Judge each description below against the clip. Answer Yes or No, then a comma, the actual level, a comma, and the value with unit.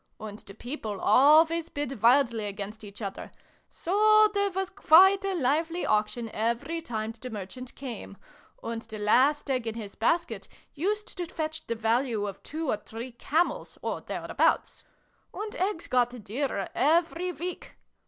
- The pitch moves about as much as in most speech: No, wide, 7.2 semitones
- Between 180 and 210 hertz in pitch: No, very high, 260 Hz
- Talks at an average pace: Yes, average, 155 wpm